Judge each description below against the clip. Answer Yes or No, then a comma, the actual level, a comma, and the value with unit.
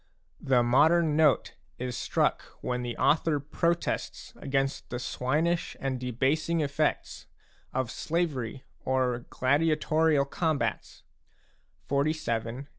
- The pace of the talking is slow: Yes, slow, 105 wpm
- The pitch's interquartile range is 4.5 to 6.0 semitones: No, average, 3.7 semitones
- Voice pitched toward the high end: No, medium, 140 Hz